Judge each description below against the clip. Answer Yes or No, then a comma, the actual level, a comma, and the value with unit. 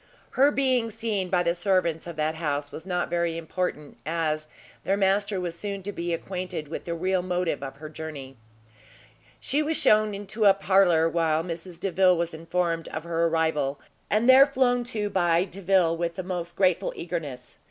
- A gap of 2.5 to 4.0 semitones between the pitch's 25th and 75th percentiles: Yes, average, 3.2 semitones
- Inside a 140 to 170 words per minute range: No, average, 180 wpm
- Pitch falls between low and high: Yes, medium, 175 Hz